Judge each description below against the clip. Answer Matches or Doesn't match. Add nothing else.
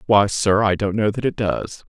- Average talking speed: Doesn't match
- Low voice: Matches